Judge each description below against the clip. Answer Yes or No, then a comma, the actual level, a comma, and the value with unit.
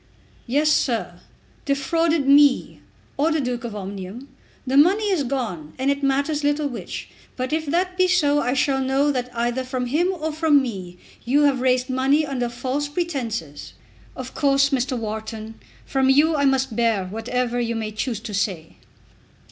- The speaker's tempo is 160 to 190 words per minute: Yes, average, 170 wpm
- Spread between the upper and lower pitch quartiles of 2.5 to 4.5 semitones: Yes, average, 3.7 semitones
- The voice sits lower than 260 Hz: No, very high, 265 Hz